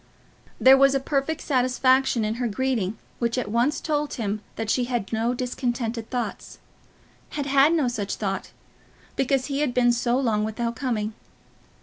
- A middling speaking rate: Yes, average, 160 wpm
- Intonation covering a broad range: No, average, 3.0 semitones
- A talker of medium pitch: No, high, 245 Hz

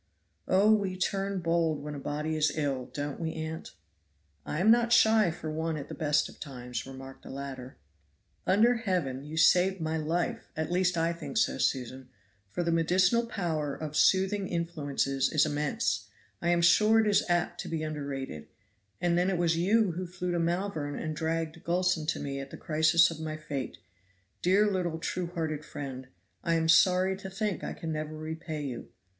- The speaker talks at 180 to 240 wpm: Yes, average, 185 wpm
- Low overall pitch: No, medium, 165 Hz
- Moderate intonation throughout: Yes, average, 3.4 semitones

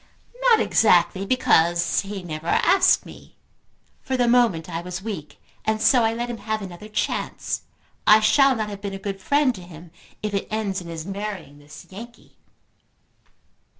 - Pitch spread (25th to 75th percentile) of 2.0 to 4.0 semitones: No, average, 4.6 semitones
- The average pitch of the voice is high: Yes, high, 200 Hz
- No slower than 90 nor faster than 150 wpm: No, average, 170 wpm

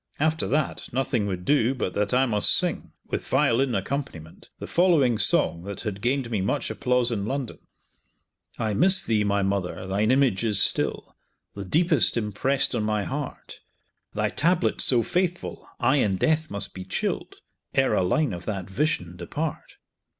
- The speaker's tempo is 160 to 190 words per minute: Yes, average, 165 wpm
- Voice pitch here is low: Yes, low, 120 Hz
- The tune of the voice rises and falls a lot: Yes, wide, 5.8 semitones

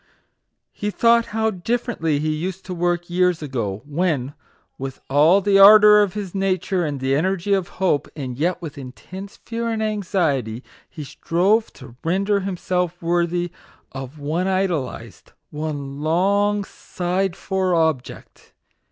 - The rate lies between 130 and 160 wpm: Yes, average, 140 wpm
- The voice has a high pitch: No, medium, 175 Hz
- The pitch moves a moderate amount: Yes, average, 4.7 semitones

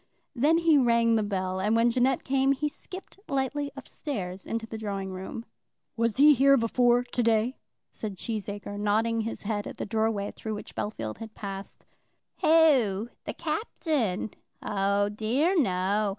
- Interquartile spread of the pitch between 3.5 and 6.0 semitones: Yes, average, 4.6 semitones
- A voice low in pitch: No, high, 225 Hz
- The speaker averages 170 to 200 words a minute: No, average, 160 wpm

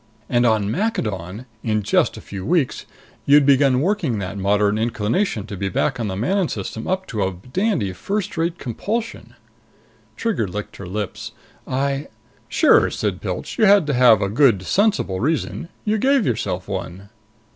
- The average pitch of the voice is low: Yes, low, 120 Hz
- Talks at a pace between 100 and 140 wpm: No, average, 170 wpm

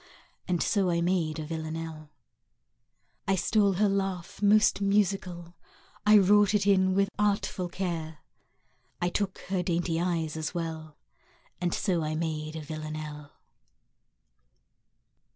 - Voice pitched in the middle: Yes, medium, 175 Hz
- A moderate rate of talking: No, slow, 125 wpm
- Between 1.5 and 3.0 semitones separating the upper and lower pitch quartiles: No, average, 3.6 semitones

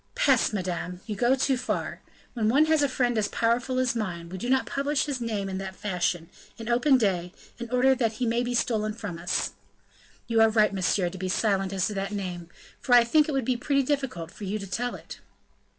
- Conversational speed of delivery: No, fast, 230 wpm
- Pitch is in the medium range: No, high, 225 Hz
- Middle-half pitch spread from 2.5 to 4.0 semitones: No, average, 4.7 semitones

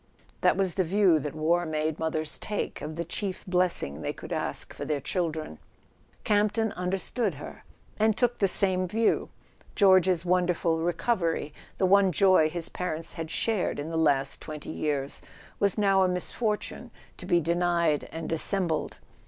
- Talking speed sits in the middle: Yes, average, 165 wpm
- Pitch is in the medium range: Yes, medium, 175 Hz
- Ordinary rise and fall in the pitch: Yes, average, 3.6 semitones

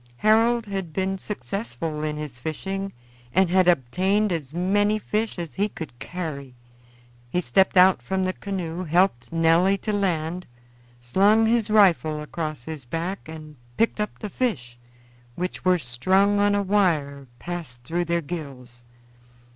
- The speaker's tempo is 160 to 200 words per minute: No, average, 145 wpm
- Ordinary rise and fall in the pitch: Yes, average, 4.5 semitones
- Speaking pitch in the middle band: Yes, medium, 175 Hz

